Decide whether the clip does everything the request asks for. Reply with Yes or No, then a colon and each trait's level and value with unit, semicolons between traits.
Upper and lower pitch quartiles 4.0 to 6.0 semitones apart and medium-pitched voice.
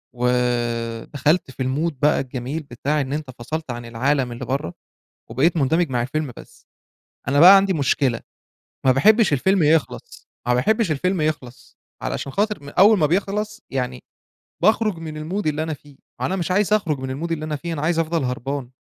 Yes: average, 4.7 semitones; medium, 150 Hz